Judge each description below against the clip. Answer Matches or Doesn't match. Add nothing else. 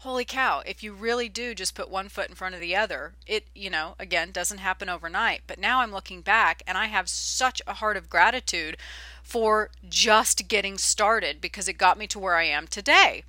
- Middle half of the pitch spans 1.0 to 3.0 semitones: Doesn't match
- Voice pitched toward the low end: Doesn't match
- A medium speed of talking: Doesn't match